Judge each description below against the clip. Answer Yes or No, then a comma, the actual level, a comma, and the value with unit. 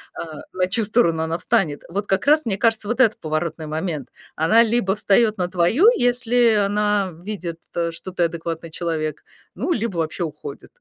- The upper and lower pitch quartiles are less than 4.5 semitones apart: No, average, 5.1 semitones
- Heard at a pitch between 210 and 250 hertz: No, high, 190 Hz